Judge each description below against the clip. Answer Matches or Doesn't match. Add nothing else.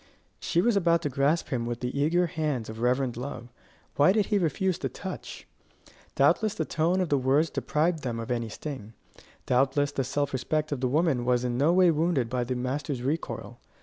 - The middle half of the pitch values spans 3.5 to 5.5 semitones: Matches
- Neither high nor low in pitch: Matches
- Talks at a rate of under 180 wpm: Doesn't match